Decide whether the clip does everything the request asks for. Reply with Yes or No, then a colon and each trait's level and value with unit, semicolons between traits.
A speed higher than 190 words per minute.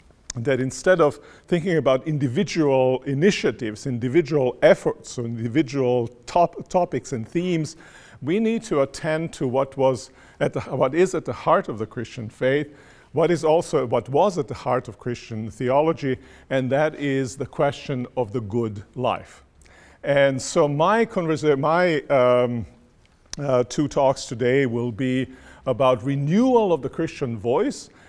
No: average, 150 wpm